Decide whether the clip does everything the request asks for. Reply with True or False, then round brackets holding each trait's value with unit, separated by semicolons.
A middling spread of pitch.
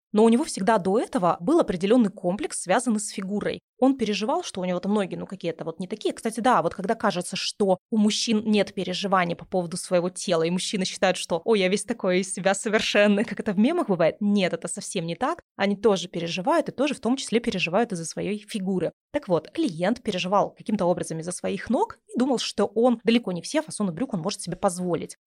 True (3.9 semitones)